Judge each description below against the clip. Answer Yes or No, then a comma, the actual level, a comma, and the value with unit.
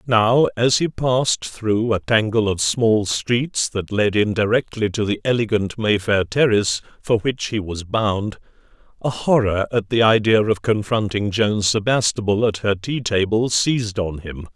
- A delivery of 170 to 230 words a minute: No, average, 160 wpm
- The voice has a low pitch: Yes, low, 110 Hz